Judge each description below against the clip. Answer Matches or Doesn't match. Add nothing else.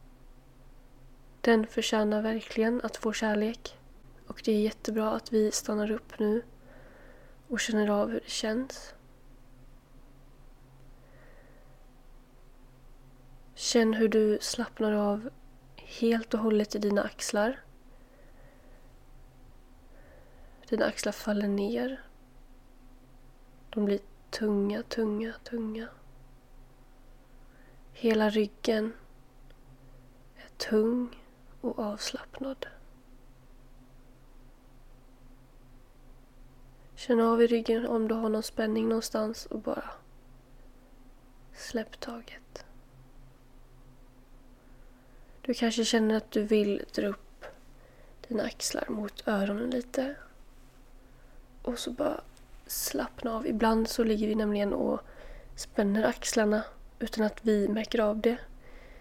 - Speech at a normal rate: Doesn't match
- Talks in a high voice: Matches